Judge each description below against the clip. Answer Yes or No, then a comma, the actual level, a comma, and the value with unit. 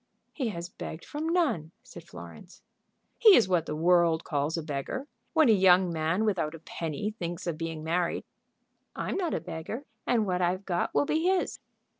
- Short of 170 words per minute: No, average, 185 wpm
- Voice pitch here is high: No, medium, 175 Hz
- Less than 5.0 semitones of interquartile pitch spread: No, average, 5.3 semitones